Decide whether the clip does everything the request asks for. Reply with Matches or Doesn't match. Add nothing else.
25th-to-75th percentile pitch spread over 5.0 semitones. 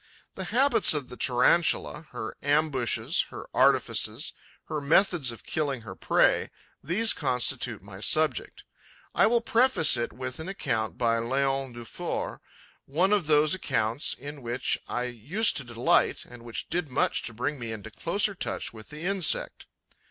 Matches